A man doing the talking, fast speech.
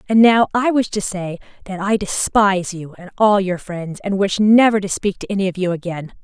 No: female; fast, 230 wpm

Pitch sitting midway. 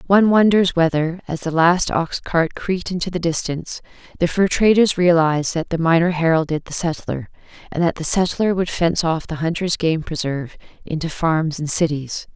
Yes: medium, 170 Hz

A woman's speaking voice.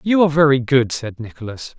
No: male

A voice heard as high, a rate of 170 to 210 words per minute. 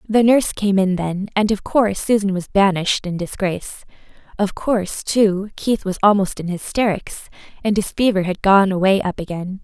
Yes: high, 195 Hz; average, 180 wpm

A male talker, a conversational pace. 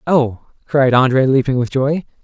Yes: male; average, 160 wpm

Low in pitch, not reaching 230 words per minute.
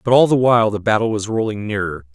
No: low, 110 Hz; fast, 250 wpm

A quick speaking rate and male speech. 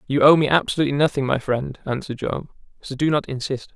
Yes: fast, 210 wpm; male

